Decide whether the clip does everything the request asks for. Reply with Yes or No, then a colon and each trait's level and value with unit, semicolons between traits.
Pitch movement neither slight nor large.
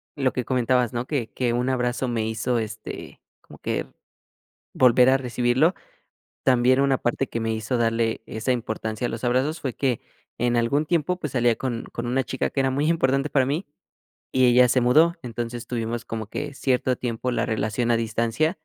No: narrow, 2.2 semitones